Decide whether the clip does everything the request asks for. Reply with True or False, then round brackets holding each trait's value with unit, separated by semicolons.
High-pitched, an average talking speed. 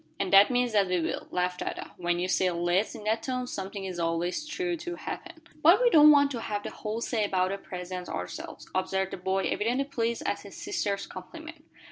False (200 Hz; 215 wpm)